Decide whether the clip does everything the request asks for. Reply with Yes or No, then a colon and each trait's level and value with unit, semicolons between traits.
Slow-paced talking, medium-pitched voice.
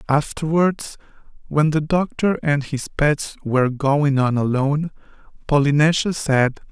Yes: slow, 115 wpm; medium, 145 Hz